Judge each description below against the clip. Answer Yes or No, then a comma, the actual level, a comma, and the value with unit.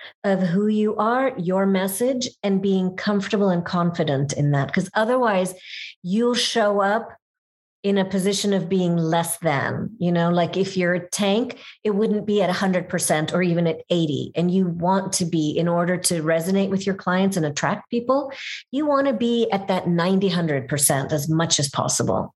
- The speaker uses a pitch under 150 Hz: No, high, 190 Hz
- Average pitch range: Yes, average, 3.3 semitones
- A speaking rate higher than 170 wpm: Yes, average, 190 wpm